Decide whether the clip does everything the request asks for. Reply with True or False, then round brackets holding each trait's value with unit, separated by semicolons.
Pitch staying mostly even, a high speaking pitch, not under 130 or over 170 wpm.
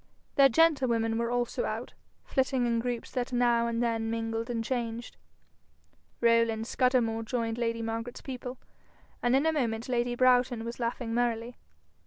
True (1.5 semitones; 235 Hz; 150 wpm)